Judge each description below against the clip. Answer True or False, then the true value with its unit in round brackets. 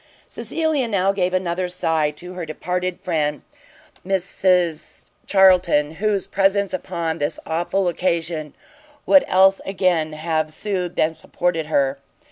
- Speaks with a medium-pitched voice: True (180 Hz)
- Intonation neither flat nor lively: True (3.0 semitones)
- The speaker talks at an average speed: False (120 wpm)